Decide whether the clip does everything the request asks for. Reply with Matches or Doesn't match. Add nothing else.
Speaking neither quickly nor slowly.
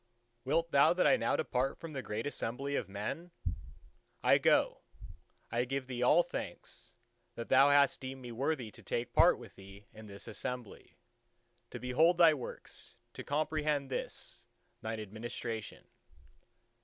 Matches